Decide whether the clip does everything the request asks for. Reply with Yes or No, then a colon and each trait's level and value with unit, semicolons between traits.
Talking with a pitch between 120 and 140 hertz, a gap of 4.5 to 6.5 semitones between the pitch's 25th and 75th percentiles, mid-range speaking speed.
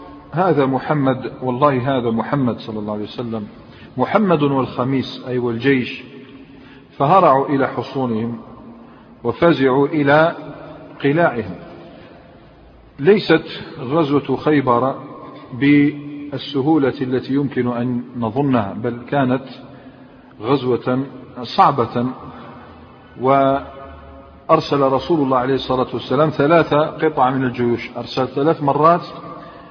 No: low, 135 Hz; average, 2.8 semitones; average, 90 wpm